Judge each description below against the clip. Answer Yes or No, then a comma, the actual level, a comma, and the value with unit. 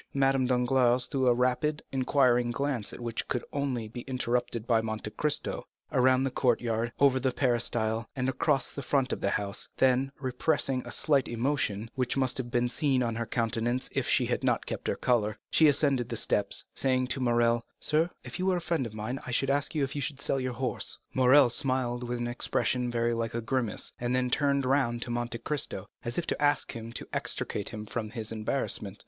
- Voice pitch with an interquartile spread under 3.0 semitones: Yes, narrow, 2.5 semitones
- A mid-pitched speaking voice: No, low, 125 Hz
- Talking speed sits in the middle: No, fast, 210 wpm